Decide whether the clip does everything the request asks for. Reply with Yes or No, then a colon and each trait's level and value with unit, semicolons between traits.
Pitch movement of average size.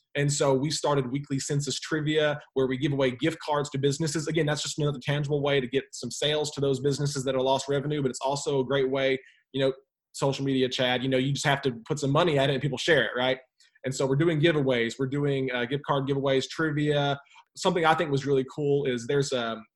No: narrow, 1.7 semitones